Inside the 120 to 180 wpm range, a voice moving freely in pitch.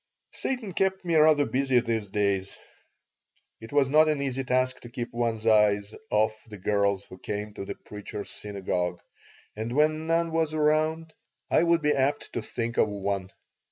Yes: average, 170 wpm; wide, 6.8 semitones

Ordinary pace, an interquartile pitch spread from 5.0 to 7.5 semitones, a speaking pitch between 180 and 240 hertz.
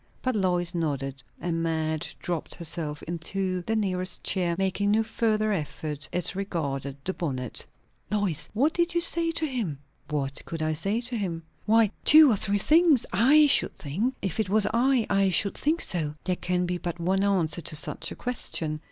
Yes: average, 185 wpm; average, 5.3 semitones; medium, 185 Hz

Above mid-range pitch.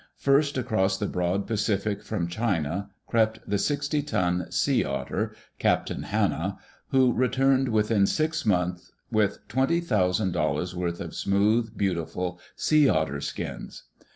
No: low, 105 Hz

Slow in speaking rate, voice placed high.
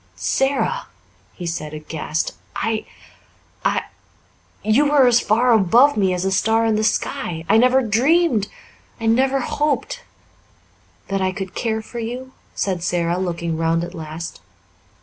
No: average, 150 wpm; high, 215 Hz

